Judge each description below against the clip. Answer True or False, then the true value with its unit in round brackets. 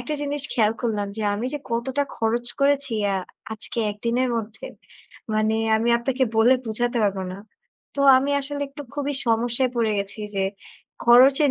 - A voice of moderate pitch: False (240 Hz)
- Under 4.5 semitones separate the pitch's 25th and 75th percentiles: True (3.7 semitones)